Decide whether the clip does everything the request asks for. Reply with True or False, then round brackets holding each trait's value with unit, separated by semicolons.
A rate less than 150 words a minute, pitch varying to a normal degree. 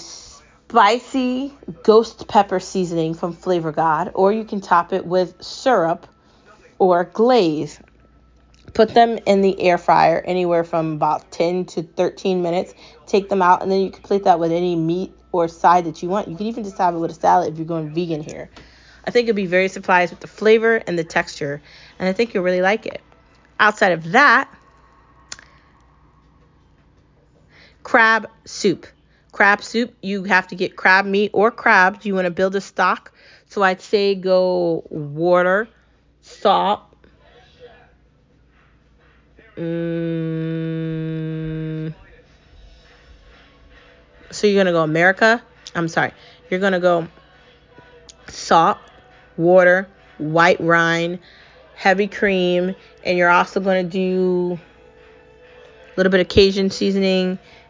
True (140 wpm; 3.1 semitones)